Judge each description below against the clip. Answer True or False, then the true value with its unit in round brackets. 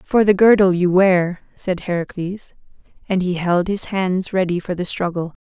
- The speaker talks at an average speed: True (175 wpm)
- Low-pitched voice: False (185 Hz)